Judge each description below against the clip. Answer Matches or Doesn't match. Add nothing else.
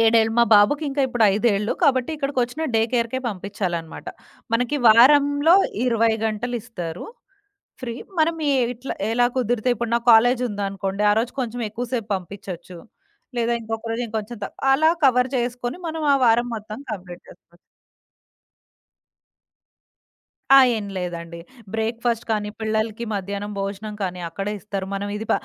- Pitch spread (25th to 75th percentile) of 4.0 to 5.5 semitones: Doesn't match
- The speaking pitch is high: Matches